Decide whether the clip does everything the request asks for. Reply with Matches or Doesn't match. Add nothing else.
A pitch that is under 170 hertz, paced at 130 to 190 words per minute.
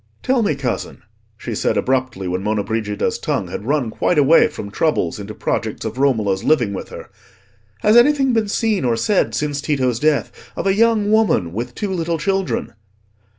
Matches